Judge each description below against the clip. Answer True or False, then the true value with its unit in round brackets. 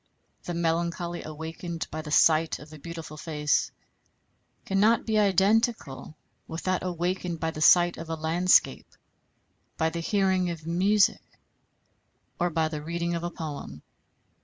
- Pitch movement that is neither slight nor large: False (2.3 semitones)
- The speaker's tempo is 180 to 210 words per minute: False (140 wpm)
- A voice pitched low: False (170 Hz)